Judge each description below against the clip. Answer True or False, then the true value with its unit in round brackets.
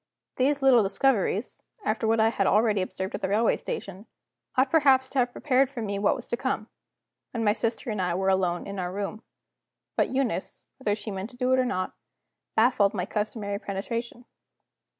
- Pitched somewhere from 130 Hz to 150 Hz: False (220 Hz)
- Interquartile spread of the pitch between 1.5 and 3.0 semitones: False (4.1 semitones)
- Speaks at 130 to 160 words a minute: False (190 wpm)